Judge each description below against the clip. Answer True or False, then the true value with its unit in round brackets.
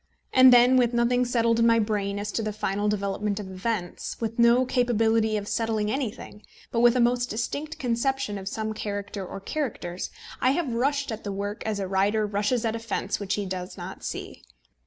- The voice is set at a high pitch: True (220 Hz)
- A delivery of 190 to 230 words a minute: True (200 wpm)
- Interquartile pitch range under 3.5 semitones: True (3.1 semitones)